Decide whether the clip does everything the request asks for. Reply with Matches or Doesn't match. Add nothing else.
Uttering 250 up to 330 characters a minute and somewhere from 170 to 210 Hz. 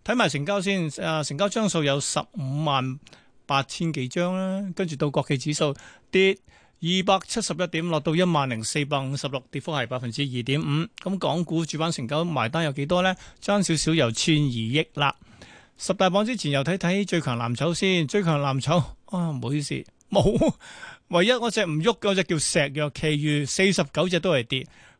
Doesn't match